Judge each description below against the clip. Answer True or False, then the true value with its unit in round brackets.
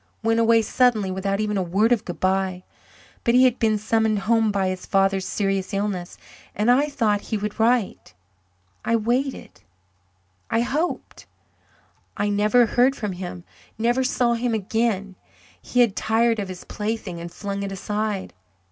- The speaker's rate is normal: True (155 wpm)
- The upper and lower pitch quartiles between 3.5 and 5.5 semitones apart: False (3.0 semitones)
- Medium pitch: False (215 Hz)